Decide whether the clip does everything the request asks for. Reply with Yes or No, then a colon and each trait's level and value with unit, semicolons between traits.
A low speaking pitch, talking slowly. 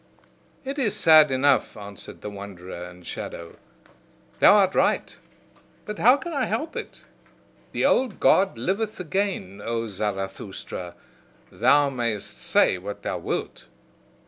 Yes: low, 130 Hz; slow, 130 wpm